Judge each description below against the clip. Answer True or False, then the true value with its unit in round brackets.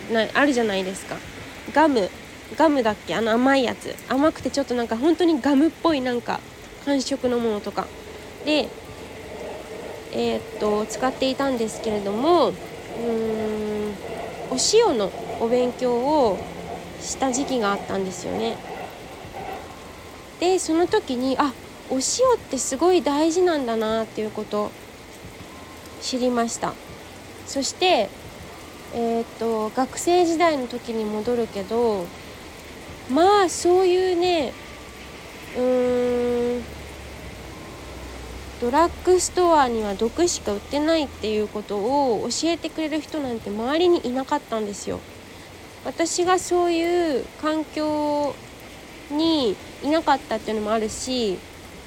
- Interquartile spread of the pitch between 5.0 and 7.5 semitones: True (6.2 semitones)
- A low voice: False (255 Hz)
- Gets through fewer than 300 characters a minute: True (250 characters per minute)